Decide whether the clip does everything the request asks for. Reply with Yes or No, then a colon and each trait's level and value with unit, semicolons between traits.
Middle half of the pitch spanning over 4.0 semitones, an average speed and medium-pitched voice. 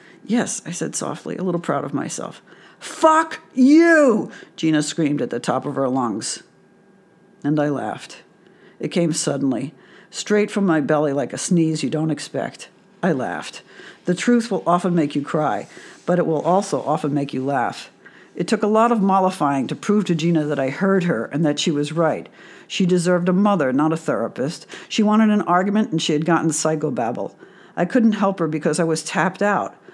Yes: average, 4.7 semitones; average, 190 wpm; medium, 170 Hz